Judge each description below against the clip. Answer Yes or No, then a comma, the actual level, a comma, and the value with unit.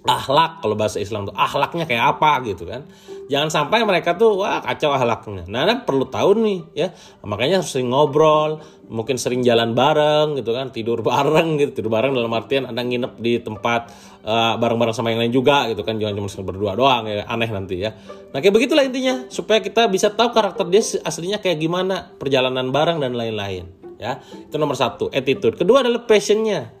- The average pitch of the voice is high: No, medium, 140 Hz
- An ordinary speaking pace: No, fast, 195 wpm